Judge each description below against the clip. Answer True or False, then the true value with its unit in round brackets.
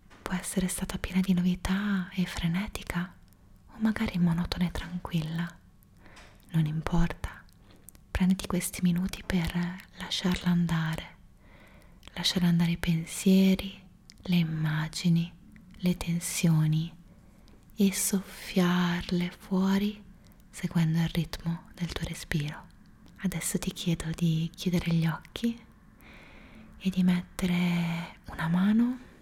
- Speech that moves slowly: True (105 wpm)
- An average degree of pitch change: False (2.2 semitones)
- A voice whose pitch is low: False (175 Hz)